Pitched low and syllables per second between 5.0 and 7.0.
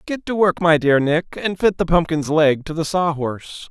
No: medium, 165 Hz; 5.1 syllables/s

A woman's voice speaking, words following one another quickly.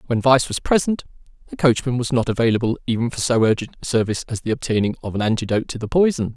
No: male; fast, 225 wpm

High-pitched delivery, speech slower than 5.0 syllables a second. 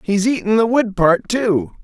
Yes: high, 200 Hz; 4.2 syllables/s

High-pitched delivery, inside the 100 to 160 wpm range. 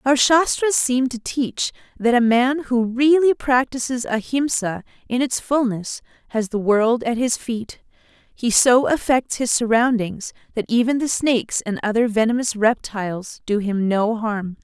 Yes: high, 235 Hz; average, 155 wpm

